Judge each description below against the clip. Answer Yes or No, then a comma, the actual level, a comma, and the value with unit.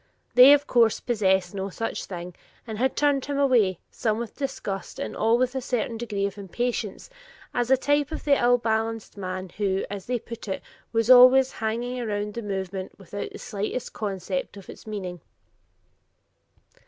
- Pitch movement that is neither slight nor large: Yes, average, 4.0 semitones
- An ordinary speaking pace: Yes, average, 175 wpm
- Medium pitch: No, high, 225 Hz